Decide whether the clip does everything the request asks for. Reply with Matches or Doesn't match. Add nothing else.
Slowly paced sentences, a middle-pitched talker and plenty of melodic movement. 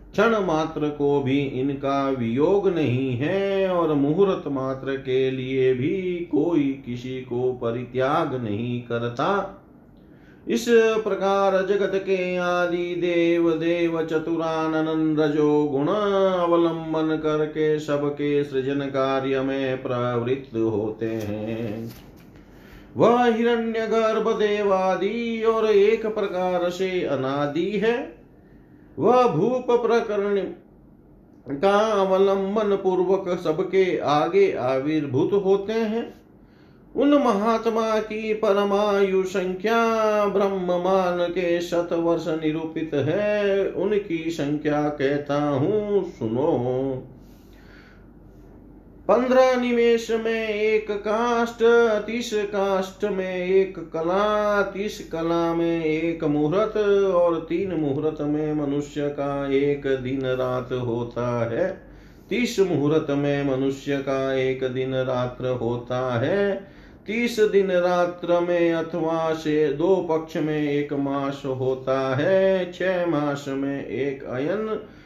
Matches